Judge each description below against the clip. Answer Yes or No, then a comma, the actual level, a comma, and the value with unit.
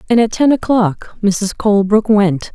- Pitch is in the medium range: No, high, 210 Hz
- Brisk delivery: No, average, 165 wpm